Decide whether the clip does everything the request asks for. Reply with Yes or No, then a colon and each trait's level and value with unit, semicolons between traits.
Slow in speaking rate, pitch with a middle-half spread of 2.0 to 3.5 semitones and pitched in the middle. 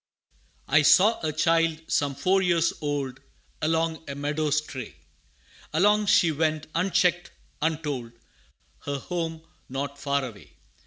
Yes: slow, 120 wpm; average, 2.7 semitones; medium, 155 Hz